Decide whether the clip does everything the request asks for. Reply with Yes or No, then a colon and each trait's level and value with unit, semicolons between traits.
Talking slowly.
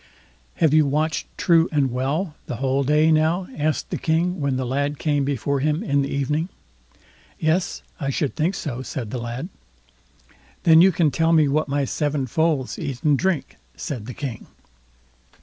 No: average, 175 wpm